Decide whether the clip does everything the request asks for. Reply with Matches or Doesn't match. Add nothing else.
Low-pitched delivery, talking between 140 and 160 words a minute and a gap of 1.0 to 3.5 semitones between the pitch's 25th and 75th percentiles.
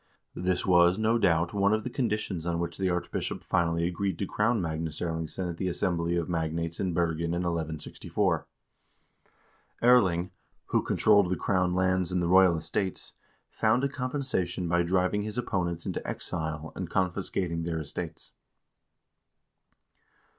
Matches